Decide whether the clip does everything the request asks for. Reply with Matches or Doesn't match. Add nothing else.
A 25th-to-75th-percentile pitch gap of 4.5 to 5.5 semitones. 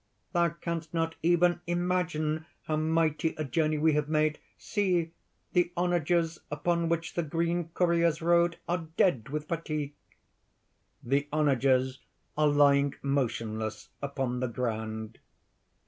Doesn't match